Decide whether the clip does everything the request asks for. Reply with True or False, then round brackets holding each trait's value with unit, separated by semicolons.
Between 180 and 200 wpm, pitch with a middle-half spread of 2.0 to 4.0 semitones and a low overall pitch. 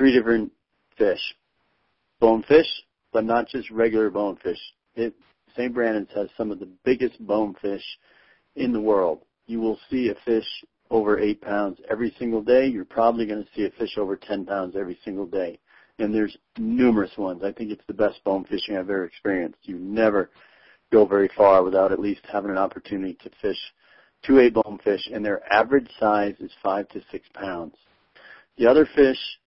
True (185 wpm; 2.7 semitones; 110 Hz)